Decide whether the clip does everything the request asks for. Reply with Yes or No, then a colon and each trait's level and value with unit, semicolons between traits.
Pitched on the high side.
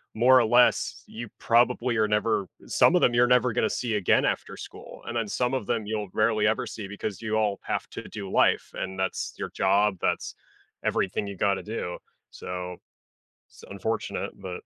No: low, 110 Hz